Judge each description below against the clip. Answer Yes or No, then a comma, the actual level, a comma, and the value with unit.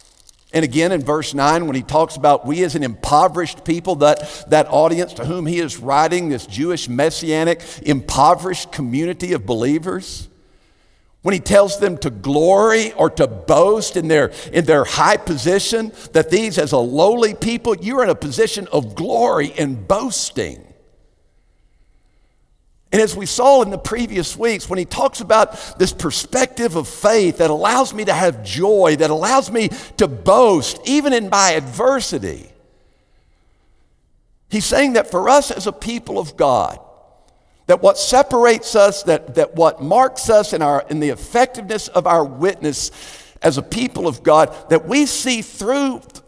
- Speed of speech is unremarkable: Yes, average, 160 wpm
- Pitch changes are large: Yes, wide, 6.9 semitones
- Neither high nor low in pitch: Yes, medium, 175 Hz